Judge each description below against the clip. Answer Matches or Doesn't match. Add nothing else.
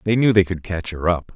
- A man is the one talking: Matches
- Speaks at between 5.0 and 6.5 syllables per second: Matches